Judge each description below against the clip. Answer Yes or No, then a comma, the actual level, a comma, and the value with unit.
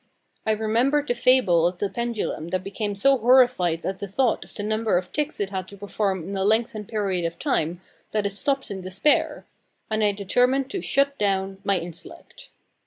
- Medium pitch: No, high, 205 Hz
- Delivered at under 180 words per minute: No, average, 195 wpm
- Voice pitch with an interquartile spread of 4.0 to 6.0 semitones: Yes, average, 4.3 semitones